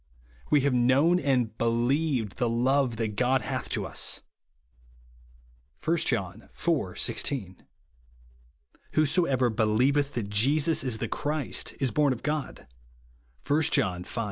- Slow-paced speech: Yes, slow, 125 wpm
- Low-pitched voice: Yes, low, 130 Hz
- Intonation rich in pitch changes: No, average, 4.3 semitones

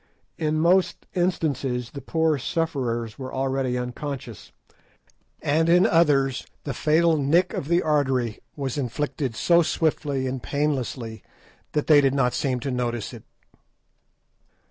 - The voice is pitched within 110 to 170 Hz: Yes, medium, 140 Hz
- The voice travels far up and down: No, average, 3.8 semitones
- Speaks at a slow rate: Yes, slow, 130 wpm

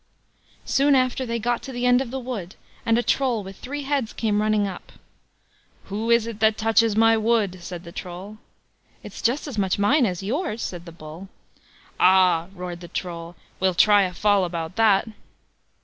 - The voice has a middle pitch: No, high, 215 Hz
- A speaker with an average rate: Yes, average, 185 wpm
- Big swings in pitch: No, average, 4.4 semitones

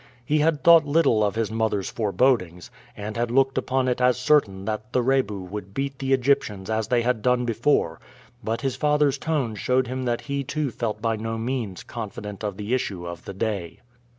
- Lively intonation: No, average, 4.1 semitones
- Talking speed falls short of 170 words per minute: No, average, 200 wpm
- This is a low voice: Yes, low, 120 Hz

